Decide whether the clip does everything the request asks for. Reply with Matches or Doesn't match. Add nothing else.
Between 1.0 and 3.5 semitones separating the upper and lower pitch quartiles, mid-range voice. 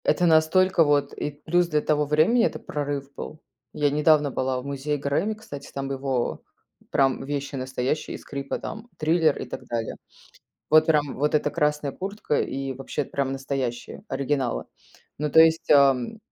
Matches